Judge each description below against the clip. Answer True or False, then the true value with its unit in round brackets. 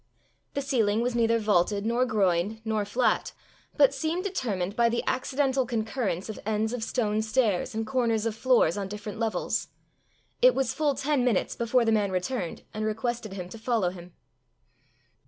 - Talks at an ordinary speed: True (170 wpm)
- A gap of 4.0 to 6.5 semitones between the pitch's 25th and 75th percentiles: False (3.3 semitones)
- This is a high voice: True (225 Hz)